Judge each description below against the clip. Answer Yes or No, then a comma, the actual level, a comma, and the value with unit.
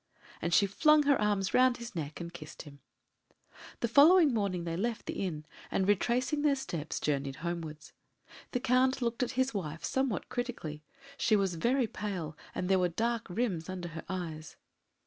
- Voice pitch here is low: No, high, 195 Hz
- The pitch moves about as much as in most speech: No, wide, 6.6 semitones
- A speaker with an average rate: Yes, average, 175 wpm